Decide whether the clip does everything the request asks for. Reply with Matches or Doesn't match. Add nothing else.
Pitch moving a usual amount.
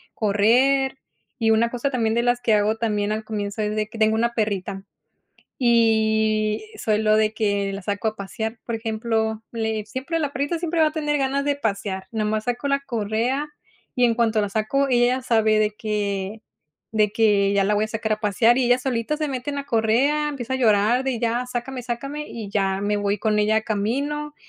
Matches